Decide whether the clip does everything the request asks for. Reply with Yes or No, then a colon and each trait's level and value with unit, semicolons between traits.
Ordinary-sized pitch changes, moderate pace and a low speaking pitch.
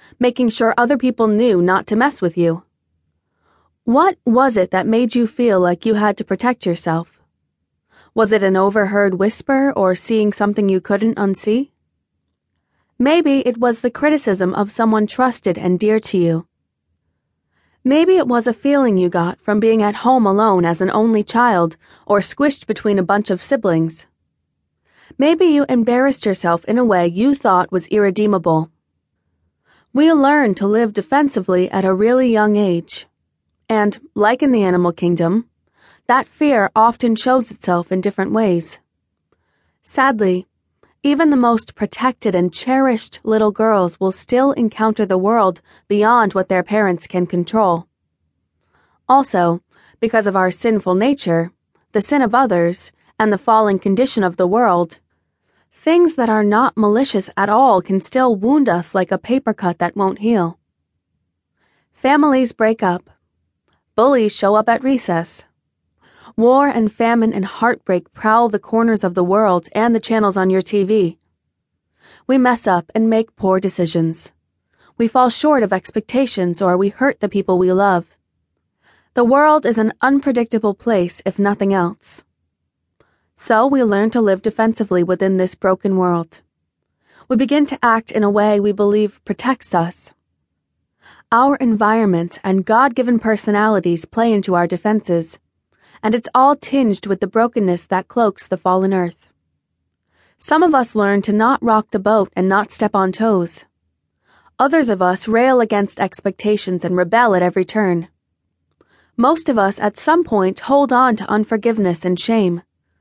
No: average, 4.5 semitones; average, 155 wpm; high, 210 Hz